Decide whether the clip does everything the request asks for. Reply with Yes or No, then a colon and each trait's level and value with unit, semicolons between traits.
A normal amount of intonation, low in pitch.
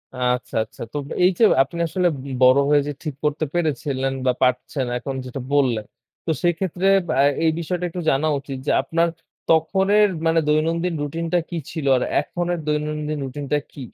No: average, 3.9 semitones; medium, 150 Hz